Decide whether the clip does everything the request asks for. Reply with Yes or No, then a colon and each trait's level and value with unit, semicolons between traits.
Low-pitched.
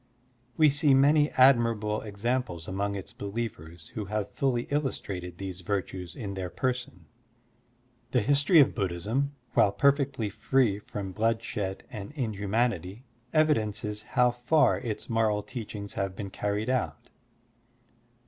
Yes: low, 110 Hz